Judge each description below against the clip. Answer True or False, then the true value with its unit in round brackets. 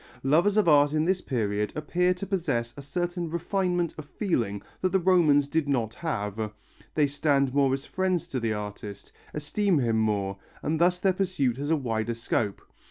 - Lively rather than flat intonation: True (7.2 semitones)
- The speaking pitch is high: False (145 Hz)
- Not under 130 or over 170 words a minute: False (180 wpm)